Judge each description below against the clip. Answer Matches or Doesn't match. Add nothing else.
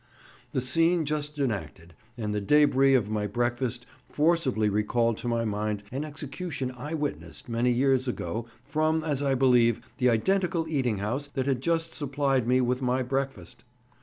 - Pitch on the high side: Doesn't match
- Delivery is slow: Doesn't match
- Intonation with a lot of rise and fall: Doesn't match